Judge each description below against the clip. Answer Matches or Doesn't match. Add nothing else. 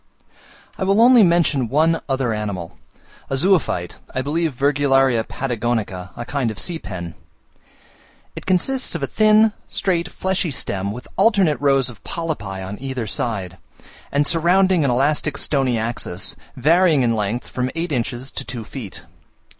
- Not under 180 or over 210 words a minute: Doesn't match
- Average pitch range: Doesn't match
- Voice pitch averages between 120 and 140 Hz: Matches